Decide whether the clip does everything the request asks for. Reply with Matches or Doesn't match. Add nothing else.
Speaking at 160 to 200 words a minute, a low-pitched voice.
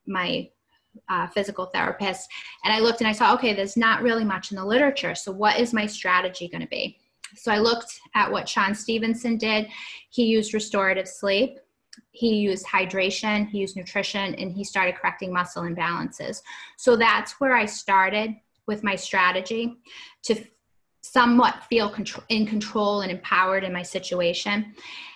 Doesn't match